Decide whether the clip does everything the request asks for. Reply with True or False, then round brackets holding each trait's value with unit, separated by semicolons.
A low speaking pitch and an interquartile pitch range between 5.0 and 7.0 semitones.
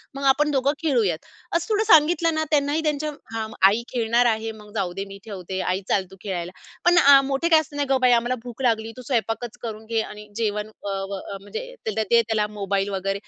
False (230 Hz; 5.6 semitones)